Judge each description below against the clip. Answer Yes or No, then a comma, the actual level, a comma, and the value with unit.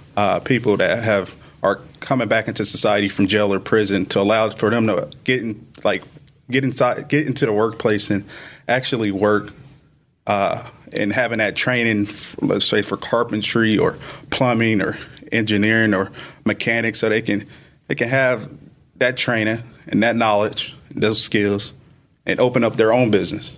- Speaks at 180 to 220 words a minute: No, average, 160 wpm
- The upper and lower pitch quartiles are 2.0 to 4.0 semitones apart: Yes, average, 3.6 semitones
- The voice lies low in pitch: Yes, low, 110 Hz